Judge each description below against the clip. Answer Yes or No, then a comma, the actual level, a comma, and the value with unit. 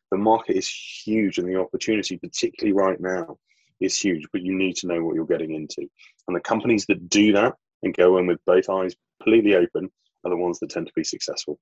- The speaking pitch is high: No, very low, 95 Hz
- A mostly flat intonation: No, average, 3.4 semitones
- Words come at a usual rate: No, fast, 220 wpm